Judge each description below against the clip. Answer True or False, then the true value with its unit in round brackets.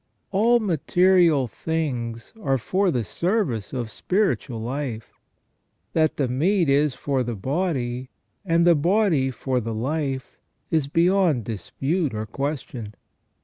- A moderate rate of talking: False (125 wpm)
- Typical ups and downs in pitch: False (6.0 semitones)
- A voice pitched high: False (140 Hz)